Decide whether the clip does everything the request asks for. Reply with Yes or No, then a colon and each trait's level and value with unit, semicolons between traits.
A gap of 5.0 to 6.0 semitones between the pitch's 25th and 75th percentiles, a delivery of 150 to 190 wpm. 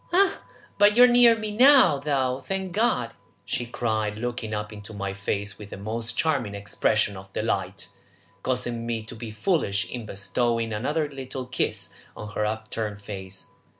Yes: wide, 5.5 semitones; average, 165 wpm